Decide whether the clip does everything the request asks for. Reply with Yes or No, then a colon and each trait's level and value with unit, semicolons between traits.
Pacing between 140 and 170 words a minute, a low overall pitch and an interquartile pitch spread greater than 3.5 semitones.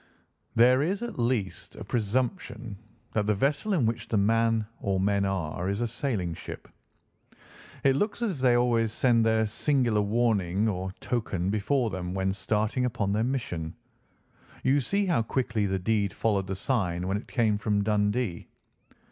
Yes: average, 165 wpm; low, 110 Hz; average, 3.9 semitones